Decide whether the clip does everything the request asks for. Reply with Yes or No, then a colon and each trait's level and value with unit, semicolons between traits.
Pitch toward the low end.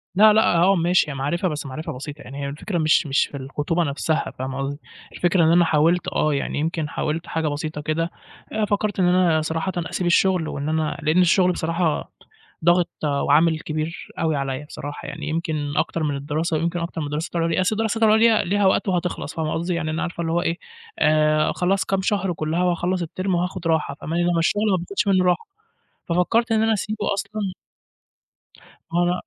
No: medium, 170 Hz